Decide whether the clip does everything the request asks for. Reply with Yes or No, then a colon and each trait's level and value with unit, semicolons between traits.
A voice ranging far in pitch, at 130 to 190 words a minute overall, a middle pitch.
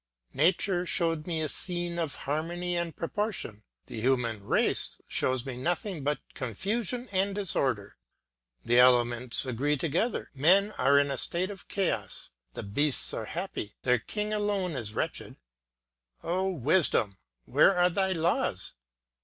Yes: wide, 6.6 semitones; average, 140 wpm; medium, 160 Hz